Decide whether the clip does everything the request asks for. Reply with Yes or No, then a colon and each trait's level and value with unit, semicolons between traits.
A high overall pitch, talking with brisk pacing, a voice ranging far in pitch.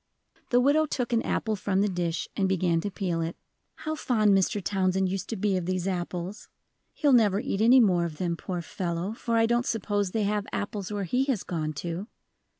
No: high, 195 Hz; fast, 210 wpm; average, 3.9 semitones